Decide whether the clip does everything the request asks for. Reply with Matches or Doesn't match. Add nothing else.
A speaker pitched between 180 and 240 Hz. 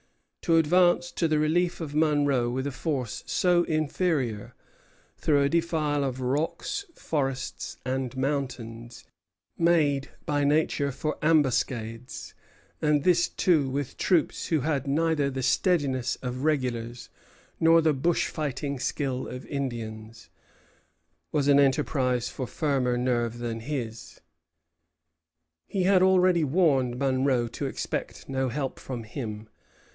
Doesn't match